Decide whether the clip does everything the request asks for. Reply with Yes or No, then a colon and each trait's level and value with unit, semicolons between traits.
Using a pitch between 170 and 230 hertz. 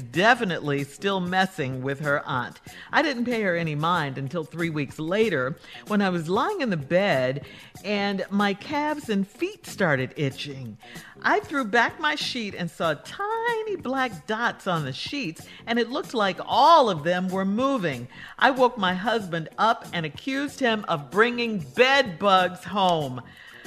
Yes: high, 190 Hz